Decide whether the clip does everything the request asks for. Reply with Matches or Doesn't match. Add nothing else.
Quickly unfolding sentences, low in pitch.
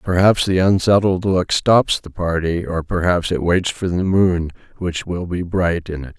Matches